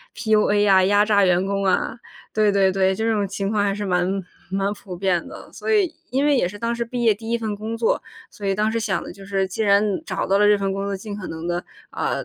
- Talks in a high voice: Yes, high, 205 Hz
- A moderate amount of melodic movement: No, narrow, 2.1 semitones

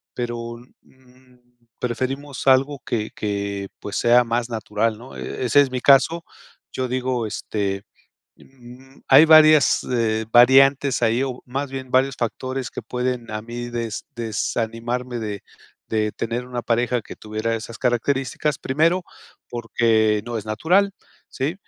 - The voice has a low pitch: Yes, low, 120 Hz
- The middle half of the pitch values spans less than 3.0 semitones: Yes, narrow, 2.6 semitones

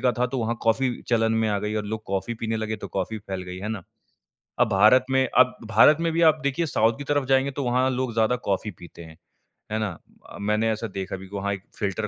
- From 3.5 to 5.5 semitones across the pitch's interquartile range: Yes, average, 3.9 semitones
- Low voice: Yes, low, 110 Hz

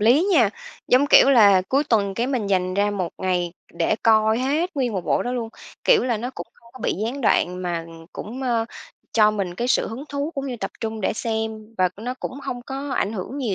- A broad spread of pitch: No, average, 4.2 semitones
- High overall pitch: Yes, high, 230 Hz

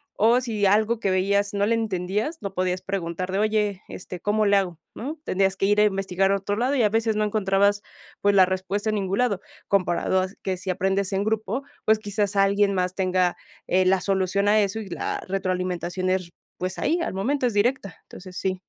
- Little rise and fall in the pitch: Yes, narrow, 2.2 semitones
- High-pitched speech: Yes, high, 195 Hz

